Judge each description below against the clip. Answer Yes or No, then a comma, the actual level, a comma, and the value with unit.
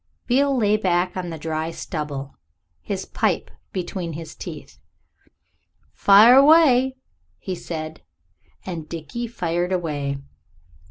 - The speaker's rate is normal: No, slow, 110 wpm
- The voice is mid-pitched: Yes, medium, 175 Hz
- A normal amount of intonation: No, wide, 5.7 semitones